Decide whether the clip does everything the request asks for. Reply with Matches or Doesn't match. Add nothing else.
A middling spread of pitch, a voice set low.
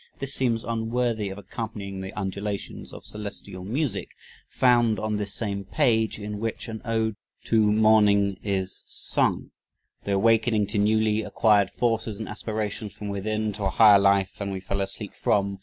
Doesn't match